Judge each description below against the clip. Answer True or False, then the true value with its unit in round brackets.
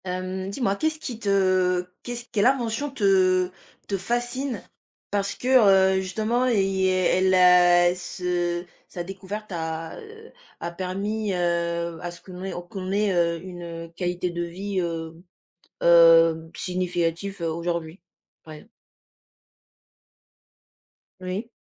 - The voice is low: False (185 Hz)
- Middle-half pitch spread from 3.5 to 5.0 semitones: False (2.7 semitones)